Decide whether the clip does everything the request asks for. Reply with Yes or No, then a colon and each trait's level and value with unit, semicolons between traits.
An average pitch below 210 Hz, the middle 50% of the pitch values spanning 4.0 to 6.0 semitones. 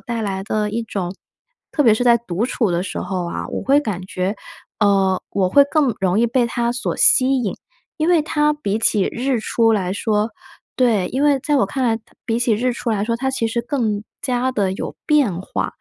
No: high, 230 Hz; average, 4.3 semitones